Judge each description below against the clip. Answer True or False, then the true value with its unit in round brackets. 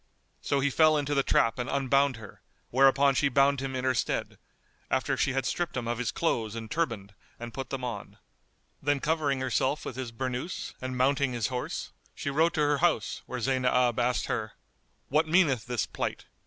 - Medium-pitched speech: False (130 Hz)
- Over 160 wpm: True (195 wpm)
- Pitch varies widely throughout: False (2.5 semitones)